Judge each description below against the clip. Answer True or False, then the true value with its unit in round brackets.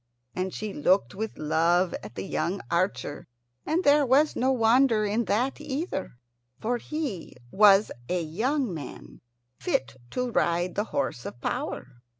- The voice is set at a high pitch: True (205 Hz)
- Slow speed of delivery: False (150 wpm)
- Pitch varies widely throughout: True (7.1 semitones)